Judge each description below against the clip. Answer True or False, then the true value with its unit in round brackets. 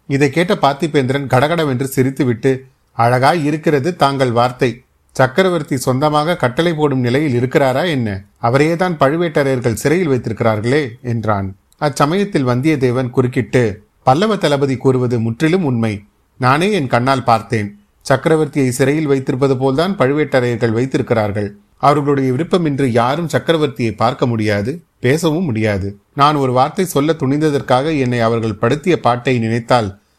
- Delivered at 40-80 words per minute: False (115 wpm)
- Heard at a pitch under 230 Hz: True (135 Hz)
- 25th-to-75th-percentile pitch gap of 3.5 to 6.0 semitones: True (4.0 semitones)